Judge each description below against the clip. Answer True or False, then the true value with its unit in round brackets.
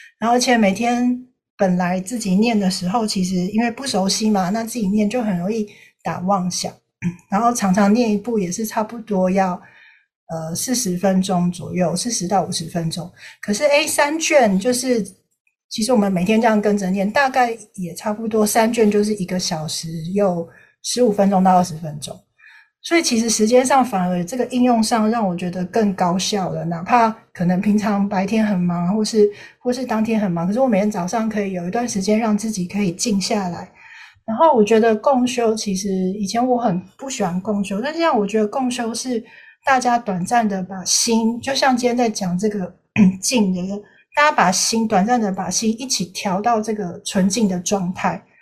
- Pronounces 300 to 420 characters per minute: False (285 characters per minute)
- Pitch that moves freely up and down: False (4.1 semitones)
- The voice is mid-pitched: False (210 Hz)